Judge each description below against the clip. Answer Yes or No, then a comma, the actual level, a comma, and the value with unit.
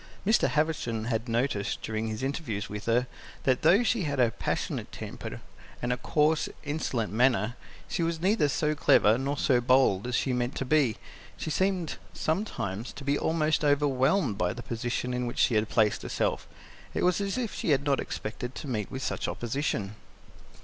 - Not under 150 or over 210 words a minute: Yes, average, 185 wpm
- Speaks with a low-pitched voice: Yes, low, 130 Hz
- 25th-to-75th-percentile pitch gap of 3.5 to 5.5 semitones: Yes, average, 4.9 semitones